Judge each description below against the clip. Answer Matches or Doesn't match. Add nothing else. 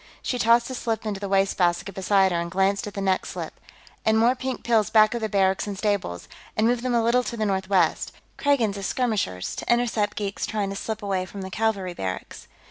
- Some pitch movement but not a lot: Matches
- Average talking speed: Doesn't match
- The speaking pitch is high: Matches